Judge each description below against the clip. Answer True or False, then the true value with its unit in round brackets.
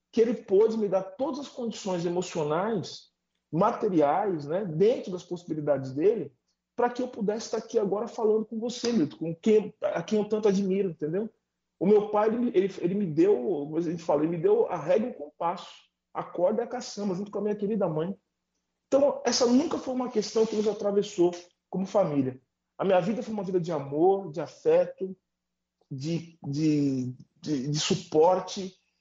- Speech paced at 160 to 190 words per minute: True (185 wpm)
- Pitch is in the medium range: False (195 Hz)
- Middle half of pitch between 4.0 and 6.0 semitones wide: True (5.1 semitones)